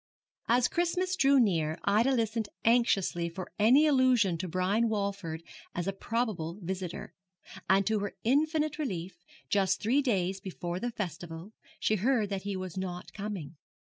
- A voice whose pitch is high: Yes, high, 200 Hz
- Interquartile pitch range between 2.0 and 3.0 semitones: No, average, 4.7 semitones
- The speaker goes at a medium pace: Yes, average, 150 wpm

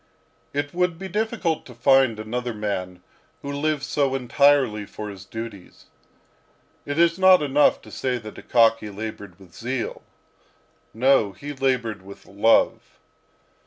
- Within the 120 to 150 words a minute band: Yes, slow, 135 wpm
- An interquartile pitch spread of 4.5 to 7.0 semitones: Yes, average, 5.2 semitones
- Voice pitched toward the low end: Yes, low, 125 Hz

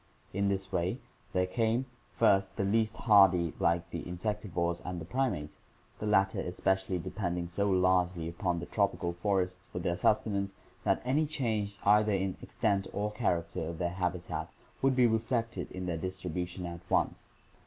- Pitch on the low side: Yes, very low, 95 Hz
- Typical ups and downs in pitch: Yes, average, 3.2 semitones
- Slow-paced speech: No, average, 160 wpm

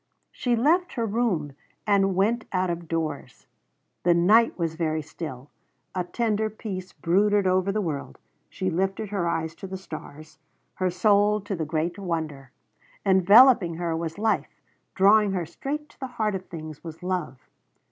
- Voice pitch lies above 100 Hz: Yes, medium, 185 Hz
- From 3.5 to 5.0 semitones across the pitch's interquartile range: Yes, average, 4.2 semitones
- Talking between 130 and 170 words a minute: Yes, average, 160 wpm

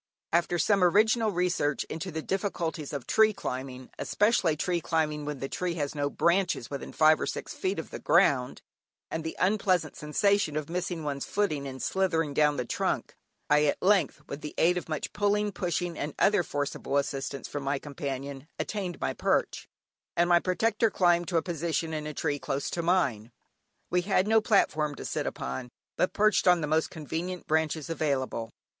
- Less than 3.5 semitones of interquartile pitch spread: No, average, 4.0 semitones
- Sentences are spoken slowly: No, average, 185 wpm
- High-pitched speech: No, medium, 160 Hz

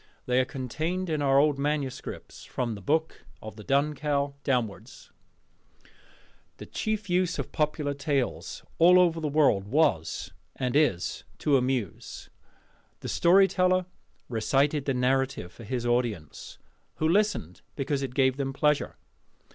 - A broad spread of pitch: No, average, 3.6 semitones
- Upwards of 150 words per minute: No, average, 140 wpm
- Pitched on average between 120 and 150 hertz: Yes, medium, 140 Hz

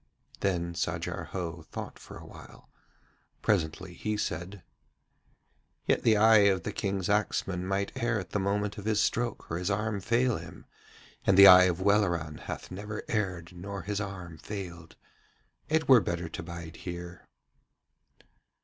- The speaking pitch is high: No, very low, 95 Hz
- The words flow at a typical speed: Yes, average, 155 wpm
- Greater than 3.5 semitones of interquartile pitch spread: No, average, 3.1 semitones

